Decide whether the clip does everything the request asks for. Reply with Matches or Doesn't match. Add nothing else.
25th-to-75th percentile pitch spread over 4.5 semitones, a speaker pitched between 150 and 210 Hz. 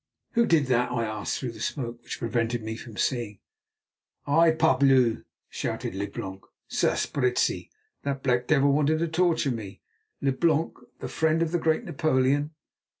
Doesn't match